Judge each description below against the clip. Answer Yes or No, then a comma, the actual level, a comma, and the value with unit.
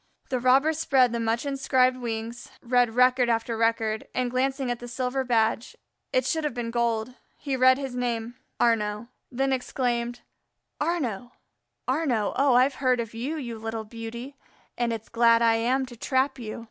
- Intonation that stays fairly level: Yes, narrow, 2.2 semitones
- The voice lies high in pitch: Yes, high, 245 Hz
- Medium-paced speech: Yes, average, 170 wpm